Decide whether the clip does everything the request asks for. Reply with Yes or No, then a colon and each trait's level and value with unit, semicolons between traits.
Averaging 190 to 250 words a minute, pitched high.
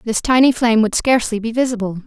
Yes: fast, 205 wpm; high, 230 Hz